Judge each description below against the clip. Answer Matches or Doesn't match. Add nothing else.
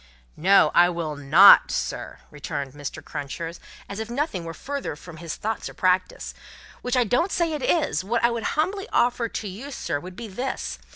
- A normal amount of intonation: Doesn't match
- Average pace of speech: Matches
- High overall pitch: Matches